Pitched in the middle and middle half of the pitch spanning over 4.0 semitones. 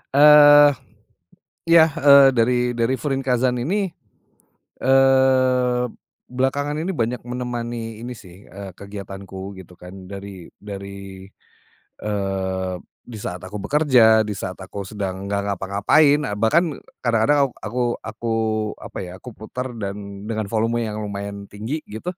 No: low, 115 Hz; average, 4.8 semitones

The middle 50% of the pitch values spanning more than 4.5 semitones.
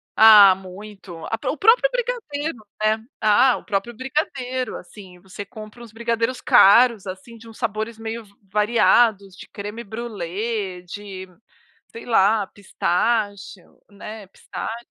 No: average, 3.0 semitones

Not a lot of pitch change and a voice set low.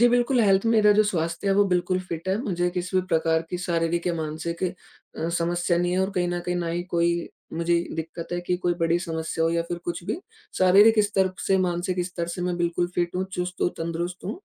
No: narrow, 1.7 semitones; medium, 175 Hz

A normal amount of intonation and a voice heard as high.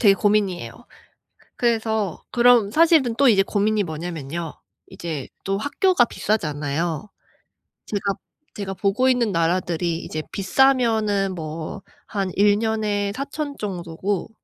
Yes: average, 4.6 semitones; high, 205 Hz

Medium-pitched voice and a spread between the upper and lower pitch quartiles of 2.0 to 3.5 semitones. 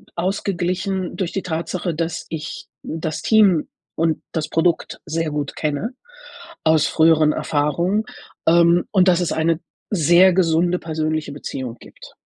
Yes: medium, 165 Hz; narrow, 2.4 semitones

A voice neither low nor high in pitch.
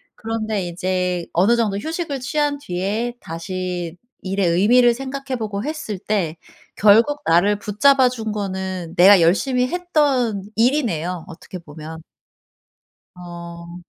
No: high, 205 Hz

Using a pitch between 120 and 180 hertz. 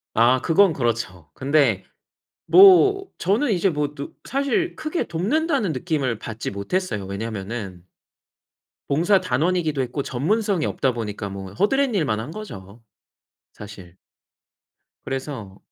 Yes: medium, 140 Hz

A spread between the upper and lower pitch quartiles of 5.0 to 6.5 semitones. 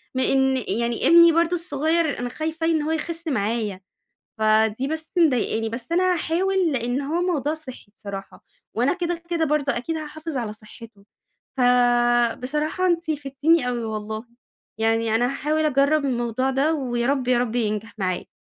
Yes: average, 5.3 semitones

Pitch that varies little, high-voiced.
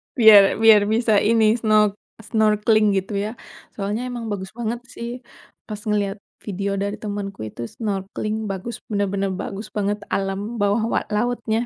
Yes: narrow, 1.9 semitones; high, 210 Hz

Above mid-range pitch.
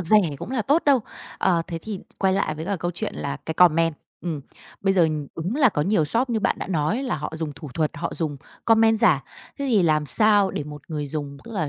No: medium, 175 Hz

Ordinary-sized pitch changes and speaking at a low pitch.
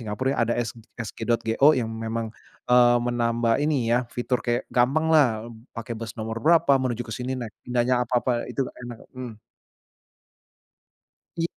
No: narrow, 1.8 semitones; low, 120 Hz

